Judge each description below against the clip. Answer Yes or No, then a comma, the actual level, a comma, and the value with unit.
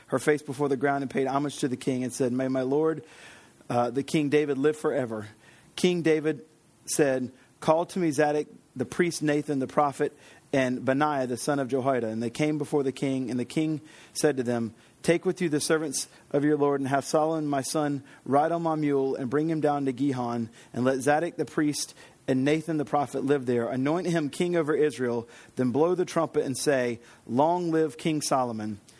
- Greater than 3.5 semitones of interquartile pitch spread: No, average, 3.1 semitones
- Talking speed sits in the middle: No, fast, 210 wpm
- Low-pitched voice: No, medium, 145 Hz